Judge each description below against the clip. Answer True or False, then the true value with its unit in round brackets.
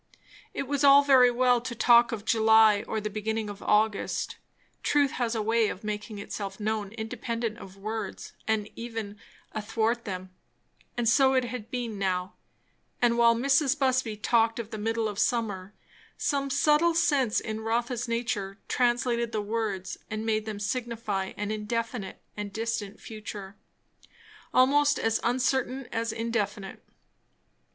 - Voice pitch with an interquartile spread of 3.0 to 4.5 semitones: False (2.6 semitones)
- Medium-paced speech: True (145 wpm)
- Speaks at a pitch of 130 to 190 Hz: False (225 Hz)